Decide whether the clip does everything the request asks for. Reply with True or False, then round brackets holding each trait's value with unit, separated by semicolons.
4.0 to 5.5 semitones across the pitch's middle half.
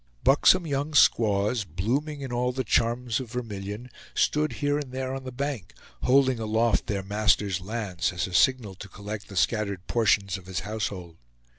True (4.7 semitones)